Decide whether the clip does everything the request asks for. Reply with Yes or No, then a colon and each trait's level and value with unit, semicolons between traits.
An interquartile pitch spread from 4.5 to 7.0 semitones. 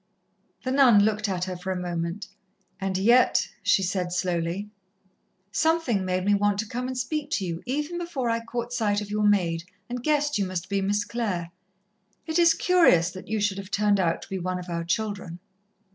Yes: average, 4.8 semitones